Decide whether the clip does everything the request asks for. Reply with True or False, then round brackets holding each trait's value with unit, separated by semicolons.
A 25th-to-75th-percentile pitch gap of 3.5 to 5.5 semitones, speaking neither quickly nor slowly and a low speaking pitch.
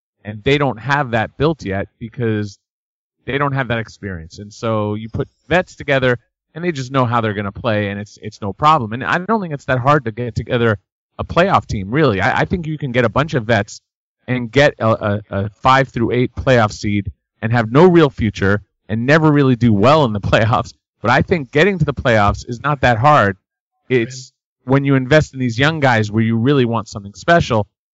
False (4.9 semitones; 225 wpm; 120 Hz)